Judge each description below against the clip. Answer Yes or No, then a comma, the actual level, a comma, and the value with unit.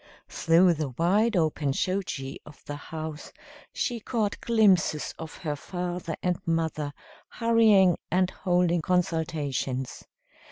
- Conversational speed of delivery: No, slow, 115 wpm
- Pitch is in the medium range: Yes, medium, 170 Hz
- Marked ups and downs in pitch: No, average, 3.4 semitones